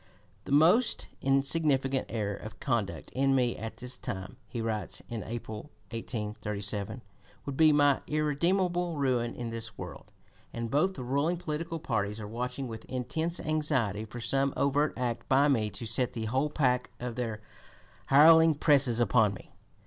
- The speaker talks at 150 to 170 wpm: Yes, average, 155 wpm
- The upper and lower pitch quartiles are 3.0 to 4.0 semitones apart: No, average, 4.5 semitones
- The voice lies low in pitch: Yes, low, 130 Hz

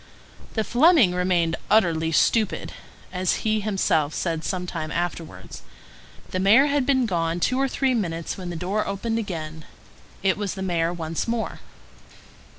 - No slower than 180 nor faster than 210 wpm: No, average, 155 wpm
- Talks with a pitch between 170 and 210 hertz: Yes, medium, 185 Hz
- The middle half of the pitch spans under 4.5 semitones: No, average, 5.0 semitones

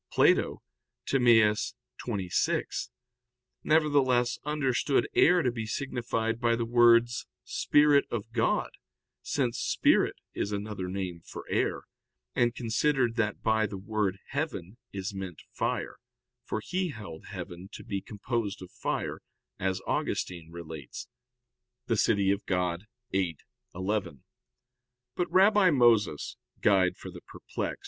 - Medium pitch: No, low, 110 Hz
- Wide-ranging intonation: No, average, 4.4 semitones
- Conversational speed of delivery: No, slow, 115 wpm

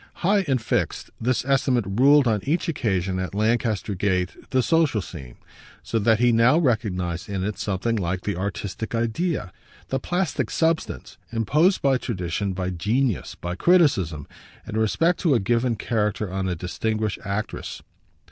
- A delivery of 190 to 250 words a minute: No, average, 155 wpm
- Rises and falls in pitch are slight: No, wide, 5.6 semitones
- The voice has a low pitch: Yes, low, 110 Hz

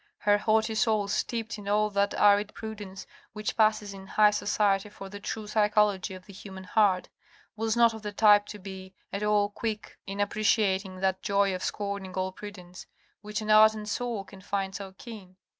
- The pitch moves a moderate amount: No, narrow, 1.7 semitones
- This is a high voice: Yes, high, 205 Hz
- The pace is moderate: Yes, average, 185 wpm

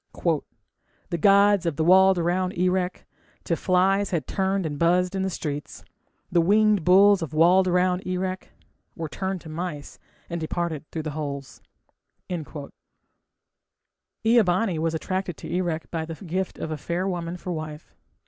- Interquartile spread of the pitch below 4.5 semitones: Yes, average, 2.7 semitones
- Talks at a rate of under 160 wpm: Yes, average, 150 wpm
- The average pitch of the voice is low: No, medium, 180 Hz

